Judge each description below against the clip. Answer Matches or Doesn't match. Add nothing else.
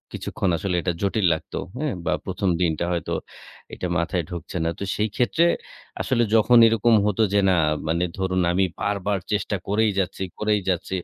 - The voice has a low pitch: Matches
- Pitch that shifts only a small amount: Doesn't match